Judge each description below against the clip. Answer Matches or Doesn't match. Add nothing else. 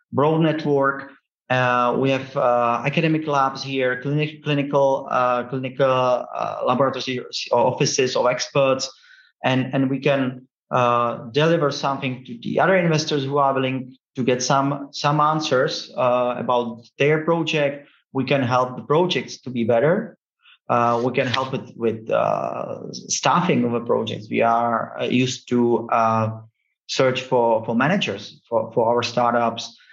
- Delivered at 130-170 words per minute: Matches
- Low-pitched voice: Matches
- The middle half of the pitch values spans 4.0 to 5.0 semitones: Doesn't match